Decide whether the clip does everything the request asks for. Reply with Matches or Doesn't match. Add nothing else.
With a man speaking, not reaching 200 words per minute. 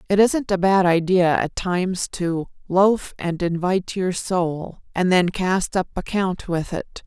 Doesn't match